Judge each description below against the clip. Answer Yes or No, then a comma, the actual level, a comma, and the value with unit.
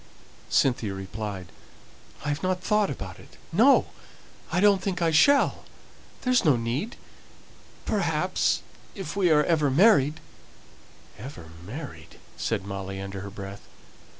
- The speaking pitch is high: No, medium, 140 Hz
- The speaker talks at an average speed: No, slow, 125 wpm